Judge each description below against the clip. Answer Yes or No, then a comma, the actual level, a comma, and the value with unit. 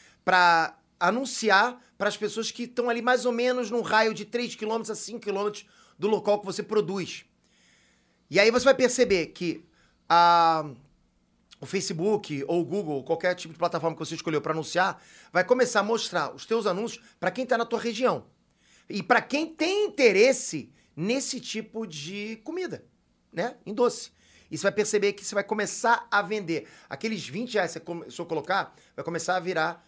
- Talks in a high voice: Yes, high, 205 Hz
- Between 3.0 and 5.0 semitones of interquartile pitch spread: No, wide, 5.4 semitones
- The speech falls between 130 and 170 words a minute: No, fast, 185 wpm